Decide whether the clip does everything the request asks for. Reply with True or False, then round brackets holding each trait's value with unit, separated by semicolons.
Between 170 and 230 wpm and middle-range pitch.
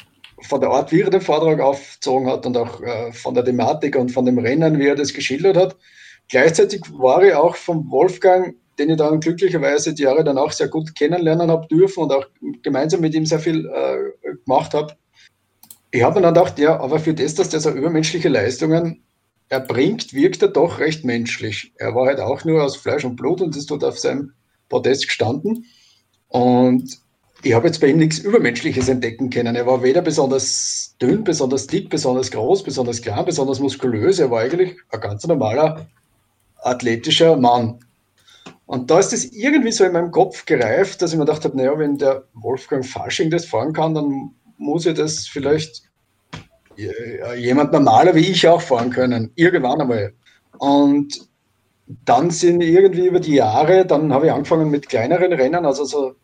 True (185 wpm; 150 Hz)